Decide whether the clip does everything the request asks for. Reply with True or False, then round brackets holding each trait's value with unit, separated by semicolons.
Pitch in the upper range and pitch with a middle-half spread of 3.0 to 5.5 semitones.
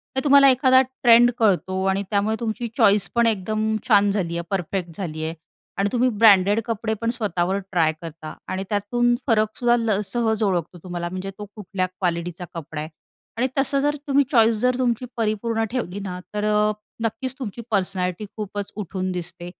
True (210 Hz; 4.0 semitones)